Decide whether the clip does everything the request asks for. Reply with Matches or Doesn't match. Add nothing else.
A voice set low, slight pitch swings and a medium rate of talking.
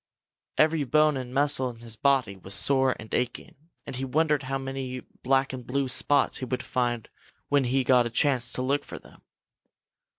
Matches